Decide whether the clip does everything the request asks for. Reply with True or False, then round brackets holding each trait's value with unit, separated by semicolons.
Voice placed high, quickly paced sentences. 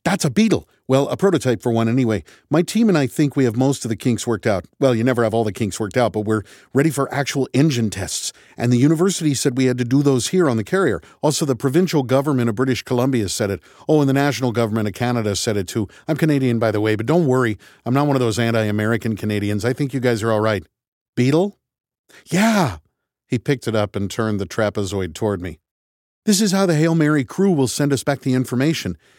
False (125 Hz; 245 wpm)